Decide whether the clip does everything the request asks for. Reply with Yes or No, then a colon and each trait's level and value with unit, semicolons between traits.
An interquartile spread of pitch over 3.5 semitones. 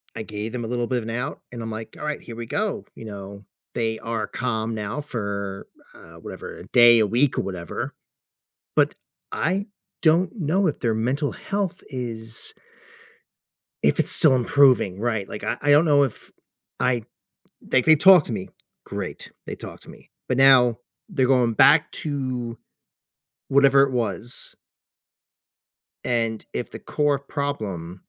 Yes: average, 4.2 semitones